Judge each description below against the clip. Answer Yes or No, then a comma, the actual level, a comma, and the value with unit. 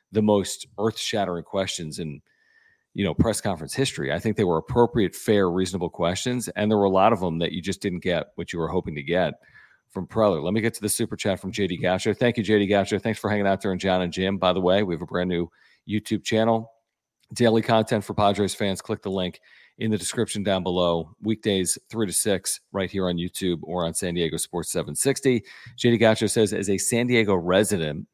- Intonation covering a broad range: No, average, 3.5 semitones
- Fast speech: Yes, fast, 225 wpm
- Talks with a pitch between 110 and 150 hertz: No, low, 100 Hz